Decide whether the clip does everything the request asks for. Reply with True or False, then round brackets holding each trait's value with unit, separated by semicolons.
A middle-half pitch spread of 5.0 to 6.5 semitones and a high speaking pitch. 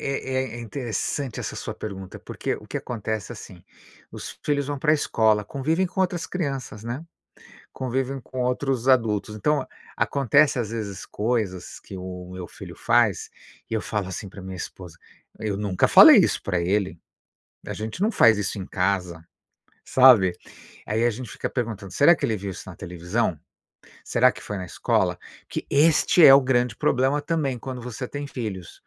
False (5.4 semitones; 115 Hz)